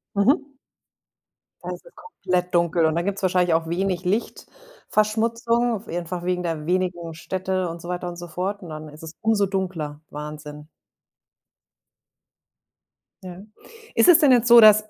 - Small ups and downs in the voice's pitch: No, average, 4.1 semitones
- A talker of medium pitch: Yes, medium, 180 Hz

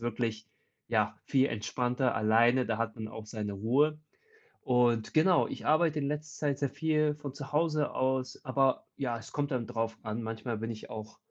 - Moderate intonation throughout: Yes, average, 4.5 semitones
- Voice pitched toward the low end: Yes, low, 125 Hz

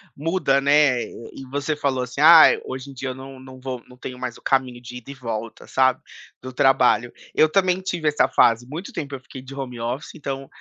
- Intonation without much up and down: Yes, narrow, 2.2 semitones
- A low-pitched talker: Yes, low, 130 Hz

